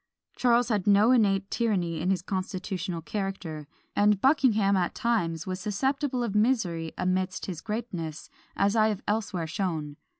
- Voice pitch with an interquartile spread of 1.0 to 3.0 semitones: No, average, 3.8 semitones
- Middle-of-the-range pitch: No, high, 195 Hz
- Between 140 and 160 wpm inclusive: Yes, average, 145 wpm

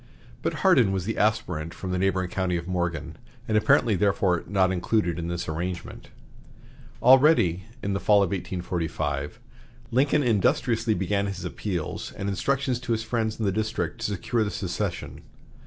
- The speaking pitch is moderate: No, low, 100 Hz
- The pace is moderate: Yes, average, 160 wpm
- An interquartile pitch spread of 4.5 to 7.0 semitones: No, average, 3.9 semitones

